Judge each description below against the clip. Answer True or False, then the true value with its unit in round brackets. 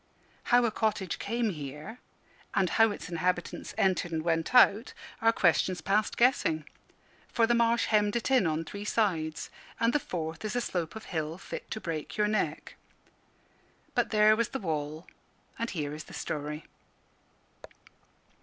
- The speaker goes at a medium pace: True (160 wpm)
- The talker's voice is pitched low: False (195 Hz)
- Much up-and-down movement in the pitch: True (5.8 semitones)